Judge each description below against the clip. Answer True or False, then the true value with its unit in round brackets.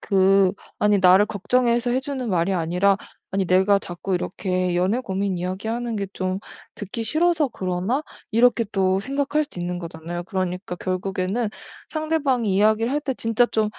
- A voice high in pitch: True (200 Hz)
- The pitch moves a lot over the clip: False (4.6 semitones)